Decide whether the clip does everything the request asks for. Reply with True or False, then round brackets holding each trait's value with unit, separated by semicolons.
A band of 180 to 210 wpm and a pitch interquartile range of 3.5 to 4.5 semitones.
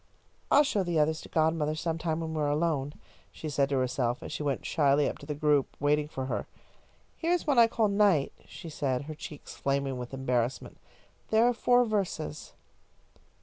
True (190 wpm; 3.9 semitones)